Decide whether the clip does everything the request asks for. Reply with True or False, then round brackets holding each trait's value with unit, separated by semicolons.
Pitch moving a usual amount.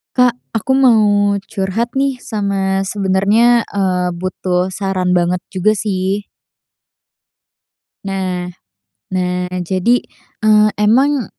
True (3.1 semitones)